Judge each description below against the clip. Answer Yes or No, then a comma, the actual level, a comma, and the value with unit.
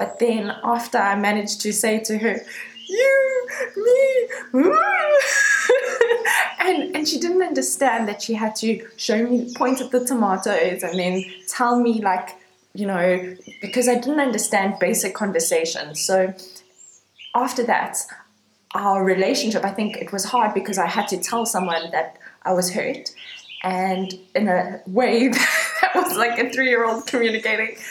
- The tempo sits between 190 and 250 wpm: No, average, 155 wpm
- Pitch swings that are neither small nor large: No, wide, 5.7 semitones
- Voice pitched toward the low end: No, high, 225 Hz